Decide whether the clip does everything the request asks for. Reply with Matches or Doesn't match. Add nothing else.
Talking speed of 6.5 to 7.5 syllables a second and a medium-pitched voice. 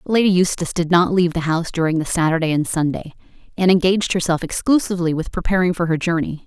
Matches